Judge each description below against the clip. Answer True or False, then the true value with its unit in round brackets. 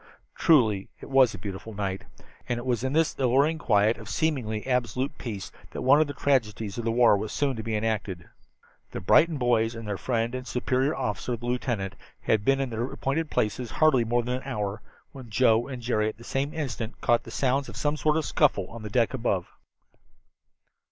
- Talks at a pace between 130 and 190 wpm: False (205 wpm)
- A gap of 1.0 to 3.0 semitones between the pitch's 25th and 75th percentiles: False (3.6 semitones)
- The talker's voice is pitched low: True (120 Hz)